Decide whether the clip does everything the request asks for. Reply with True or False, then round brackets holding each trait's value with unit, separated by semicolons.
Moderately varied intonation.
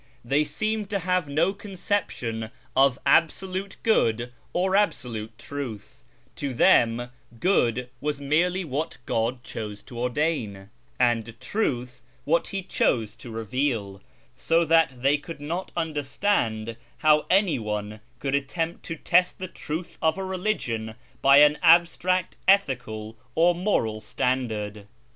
False (7.3 semitones)